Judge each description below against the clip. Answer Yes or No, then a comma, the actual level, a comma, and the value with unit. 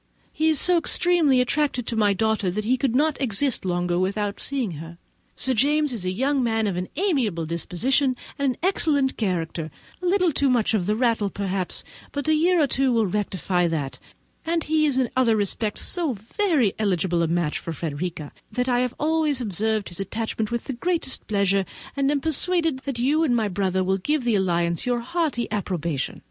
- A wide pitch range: Yes, wide, 6.9 semitones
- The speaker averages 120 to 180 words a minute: No, average, 195 wpm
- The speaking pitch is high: Yes, high, 230 Hz